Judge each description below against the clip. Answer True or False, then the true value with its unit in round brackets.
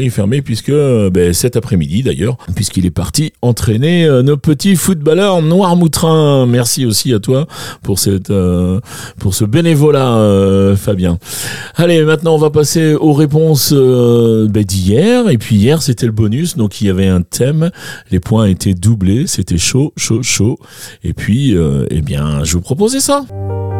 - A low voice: True (120 Hz)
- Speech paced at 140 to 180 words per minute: True (170 wpm)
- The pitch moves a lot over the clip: True (7.6 semitones)